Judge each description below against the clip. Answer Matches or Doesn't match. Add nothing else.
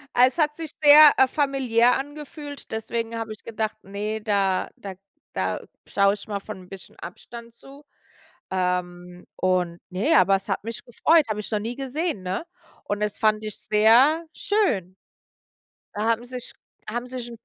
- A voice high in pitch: Matches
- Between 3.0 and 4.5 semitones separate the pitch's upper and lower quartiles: Doesn't match